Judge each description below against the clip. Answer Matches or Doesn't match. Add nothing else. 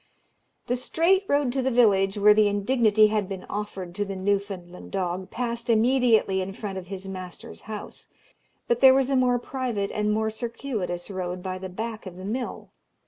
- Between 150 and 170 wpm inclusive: Doesn't match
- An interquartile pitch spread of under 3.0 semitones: Doesn't match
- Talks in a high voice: Matches